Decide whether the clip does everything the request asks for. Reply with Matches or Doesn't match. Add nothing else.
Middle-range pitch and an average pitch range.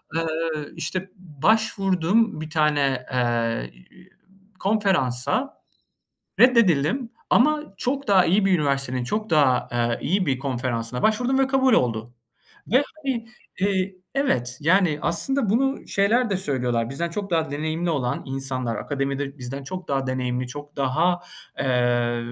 Doesn't match